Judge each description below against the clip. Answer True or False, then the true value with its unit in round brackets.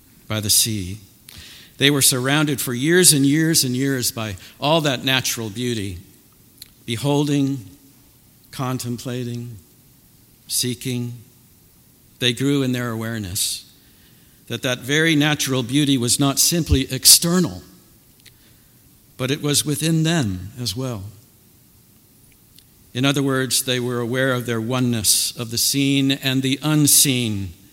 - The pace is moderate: False (120 wpm)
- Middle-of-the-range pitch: False (125 Hz)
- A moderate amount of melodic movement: True (3.0 semitones)